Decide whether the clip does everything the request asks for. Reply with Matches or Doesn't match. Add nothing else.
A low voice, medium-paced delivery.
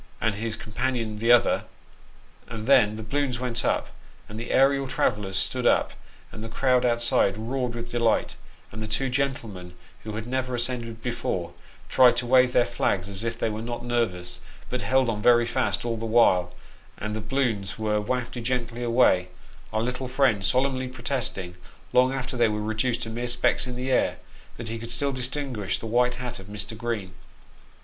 Matches